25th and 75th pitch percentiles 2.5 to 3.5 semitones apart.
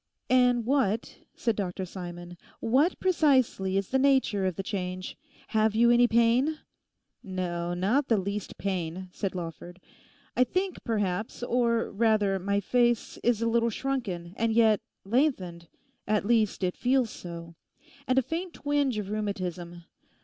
No: average, 4.8 semitones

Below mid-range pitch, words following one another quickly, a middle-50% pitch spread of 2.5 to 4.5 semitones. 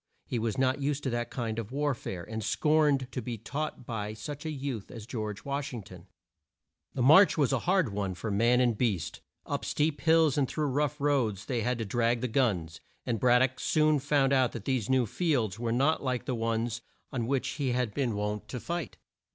Yes: low, 125 Hz; fast, 220 wpm; average, 4.0 semitones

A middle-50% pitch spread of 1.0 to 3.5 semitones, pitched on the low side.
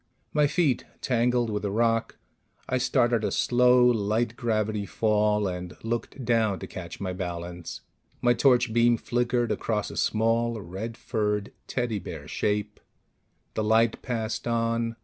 Yes: narrow, 2.4 semitones; low, 115 Hz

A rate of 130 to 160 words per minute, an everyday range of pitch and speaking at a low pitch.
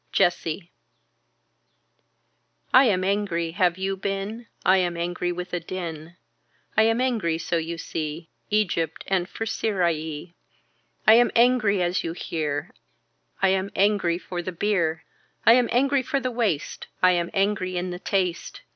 No: average, 150 wpm; average, 3.6 semitones; medium, 185 Hz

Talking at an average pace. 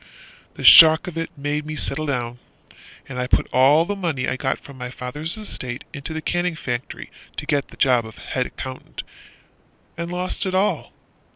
Yes: average, 185 wpm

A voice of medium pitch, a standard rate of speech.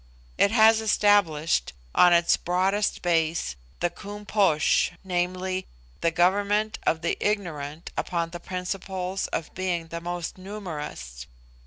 No: medium, 180 Hz; slow, 125 wpm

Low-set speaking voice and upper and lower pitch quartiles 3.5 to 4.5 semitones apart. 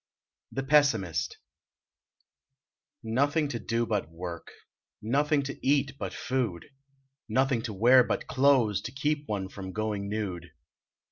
No: low, 115 Hz; wide, 5.6 semitones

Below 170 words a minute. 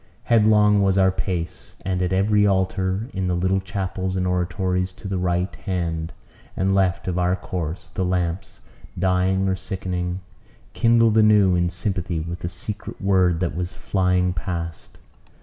Yes: average, 155 wpm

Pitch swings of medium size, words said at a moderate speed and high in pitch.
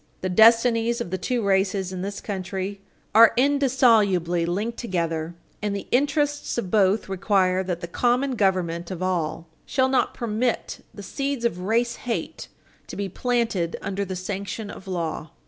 Yes: average, 4.3 semitones; average, 160 wpm; high, 200 Hz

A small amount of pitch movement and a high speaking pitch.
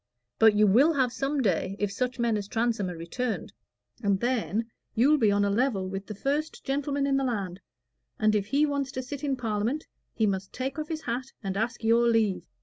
No: average, 4.9 semitones; high, 235 Hz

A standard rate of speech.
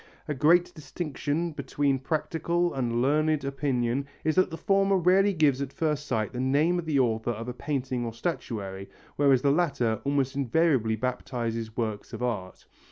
Yes: average, 165 wpm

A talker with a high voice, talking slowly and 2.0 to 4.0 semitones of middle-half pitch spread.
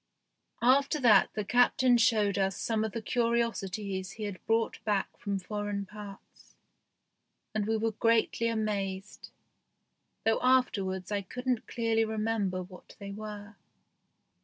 Yes: high, 215 Hz; slow, 125 wpm; narrow, 2.5 semitones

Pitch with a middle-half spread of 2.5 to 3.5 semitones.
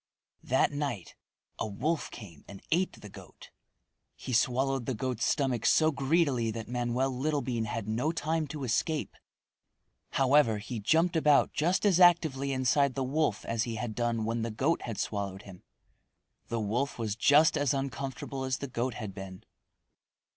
No: average, 4.2 semitones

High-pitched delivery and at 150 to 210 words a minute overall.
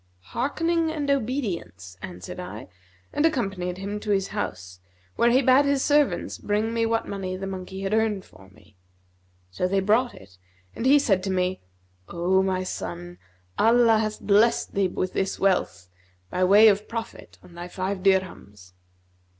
Yes: high, 195 Hz; average, 165 wpm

